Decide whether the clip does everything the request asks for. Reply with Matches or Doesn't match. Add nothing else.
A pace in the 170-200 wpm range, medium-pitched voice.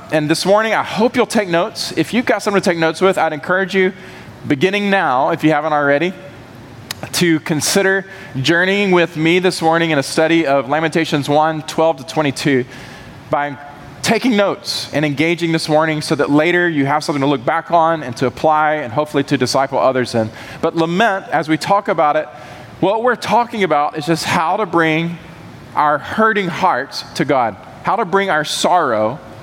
Matches